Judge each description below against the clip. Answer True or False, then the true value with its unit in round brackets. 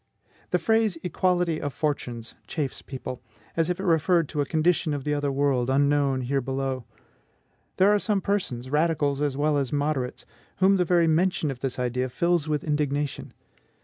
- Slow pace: False (175 wpm)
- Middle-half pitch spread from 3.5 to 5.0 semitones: True (4.1 semitones)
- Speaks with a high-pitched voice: False (145 Hz)